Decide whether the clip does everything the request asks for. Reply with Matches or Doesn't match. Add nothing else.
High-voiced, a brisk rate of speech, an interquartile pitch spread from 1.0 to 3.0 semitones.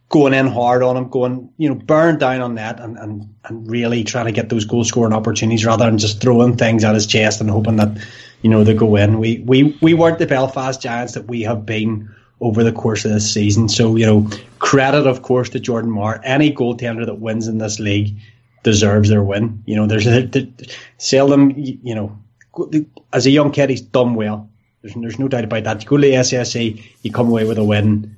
Doesn't match